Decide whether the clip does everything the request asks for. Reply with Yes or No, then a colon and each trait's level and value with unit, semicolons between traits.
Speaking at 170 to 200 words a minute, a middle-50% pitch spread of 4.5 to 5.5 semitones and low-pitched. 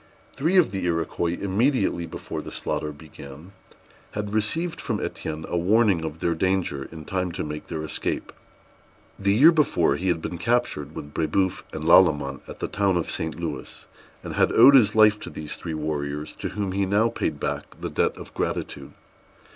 Yes: average, 185 wpm; average, 5.0 semitones; very low, 90 Hz